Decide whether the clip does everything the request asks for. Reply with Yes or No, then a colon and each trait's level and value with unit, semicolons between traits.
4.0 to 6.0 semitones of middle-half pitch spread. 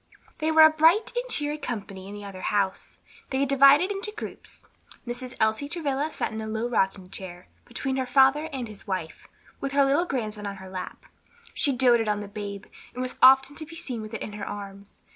Yes: wide, 5.6 semitones